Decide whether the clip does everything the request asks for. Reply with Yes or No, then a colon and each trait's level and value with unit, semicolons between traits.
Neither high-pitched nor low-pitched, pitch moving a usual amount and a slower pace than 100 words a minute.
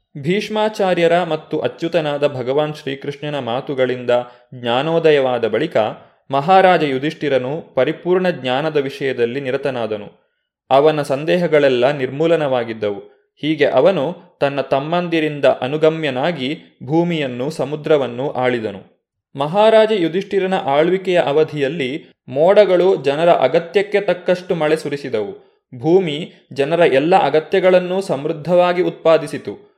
Yes: medium, 155 Hz; average, 4.8 semitones; average, 85 wpm